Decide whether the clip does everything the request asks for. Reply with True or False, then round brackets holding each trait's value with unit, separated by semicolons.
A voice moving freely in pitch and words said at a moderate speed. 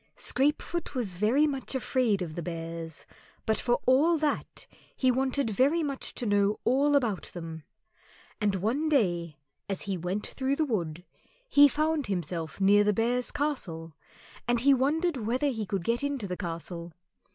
True (7.4 semitones; 165 wpm)